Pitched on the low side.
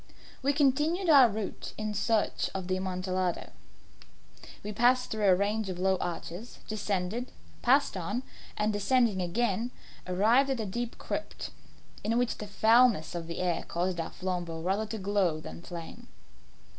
No: high, 205 Hz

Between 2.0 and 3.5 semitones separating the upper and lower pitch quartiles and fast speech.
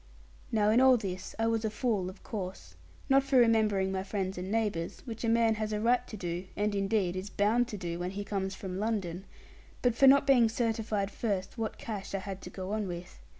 Yes: average, 3.1 semitones; fast, 225 wpm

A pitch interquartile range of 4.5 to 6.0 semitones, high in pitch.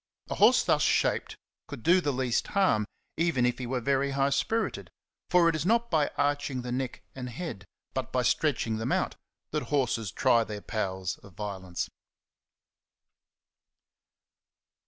No: average, 4.9 semitones; low, 130 Hz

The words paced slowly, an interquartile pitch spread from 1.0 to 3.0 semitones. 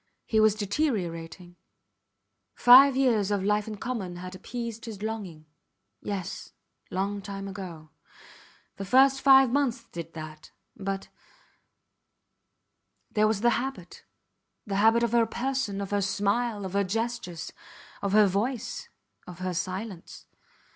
No: slow, 130 wpm; average, 3.8 semitones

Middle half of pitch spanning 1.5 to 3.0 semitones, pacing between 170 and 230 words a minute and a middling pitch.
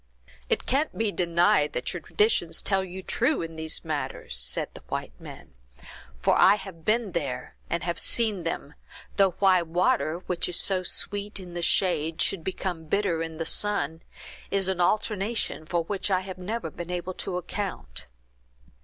No: average, 3.4 semitones; average, 175 wpm; medium, 180 Hz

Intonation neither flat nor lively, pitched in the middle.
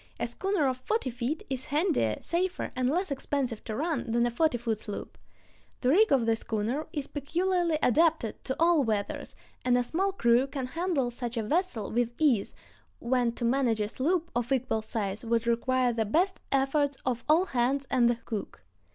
No: average, 4.9 semitones; very high, 255 Hz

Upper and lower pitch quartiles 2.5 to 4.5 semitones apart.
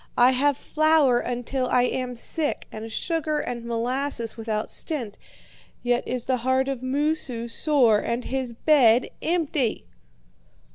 Yes: average, 3.4 semitones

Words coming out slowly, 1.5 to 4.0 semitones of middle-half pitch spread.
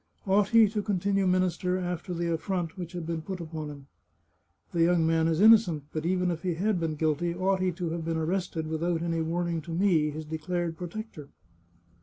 No: fast, 205 wpm; narrow, 2.4 semitones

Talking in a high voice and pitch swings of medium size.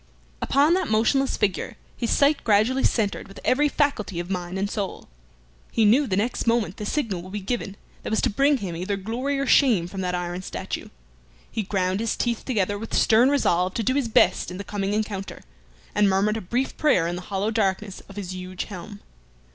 Yes: high, 210 Hz; average, 4.2 semitones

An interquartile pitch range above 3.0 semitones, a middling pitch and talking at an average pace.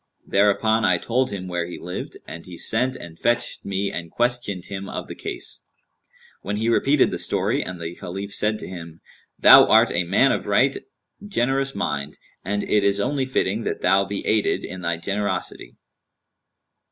No: average, 4.4 semitones; low, 100 Hz; average, 175 wpm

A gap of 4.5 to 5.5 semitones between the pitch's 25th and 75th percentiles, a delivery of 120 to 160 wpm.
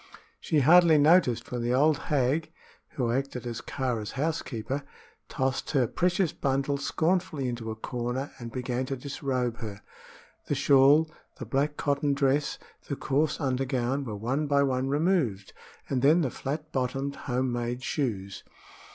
No: average, 3.0 semitones; average, 150 wpm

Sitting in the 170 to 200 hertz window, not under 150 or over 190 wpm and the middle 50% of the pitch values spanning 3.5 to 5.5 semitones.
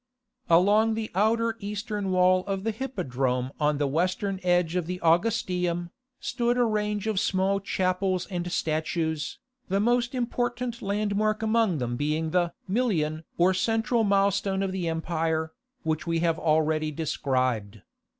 No: medium, 185 Hz; average, 140 wpm; average, 4.7 semitones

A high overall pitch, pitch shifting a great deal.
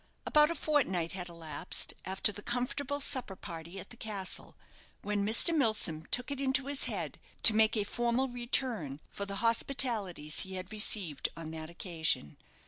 Yes: high, 210 Hz; wide, 6.2 semitones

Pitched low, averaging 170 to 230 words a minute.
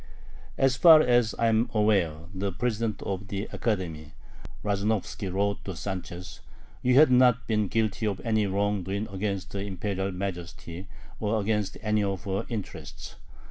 No: low, 100 Hz; average, 150 wpm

